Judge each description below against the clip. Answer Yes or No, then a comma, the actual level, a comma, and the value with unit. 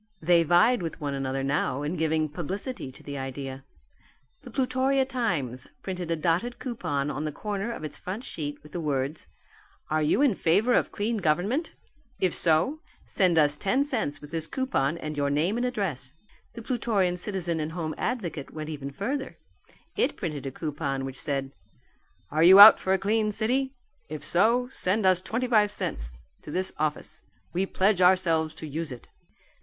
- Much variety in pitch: Yes, wide, 6.5 semitones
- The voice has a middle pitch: Yes, medium, 170 Hz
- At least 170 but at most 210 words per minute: Yes, average, 180 wpm